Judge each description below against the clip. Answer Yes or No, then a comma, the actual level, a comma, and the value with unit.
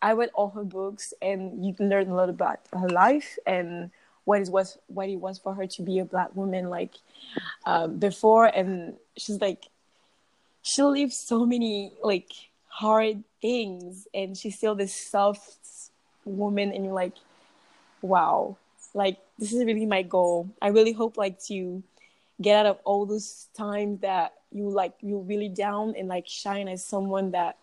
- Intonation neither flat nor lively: No, narrow, 2.0 semitones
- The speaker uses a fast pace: No, average, 175 wpm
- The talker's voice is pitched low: No, high, 200 Hz